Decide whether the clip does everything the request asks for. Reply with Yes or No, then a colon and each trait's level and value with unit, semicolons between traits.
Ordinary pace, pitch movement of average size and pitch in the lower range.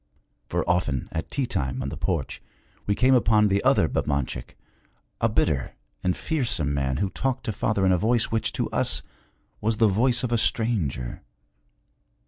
No: average, 170 wpm; wide, 7.9 semitones; low, 105 Hz